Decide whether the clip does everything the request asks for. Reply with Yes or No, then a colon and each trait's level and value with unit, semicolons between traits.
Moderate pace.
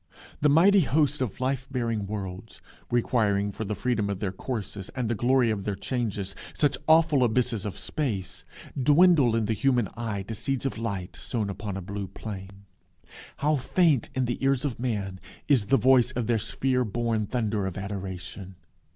Yes: average, 175 wpm